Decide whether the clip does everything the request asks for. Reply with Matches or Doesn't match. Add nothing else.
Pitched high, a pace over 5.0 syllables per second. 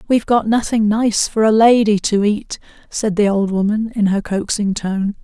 Doesn't match